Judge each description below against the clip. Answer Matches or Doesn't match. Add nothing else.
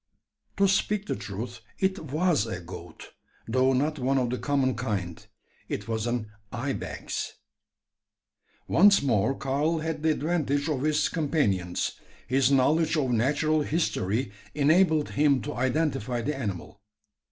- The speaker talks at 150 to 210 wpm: Doesn't match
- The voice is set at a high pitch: Doesn't match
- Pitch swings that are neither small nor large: Matches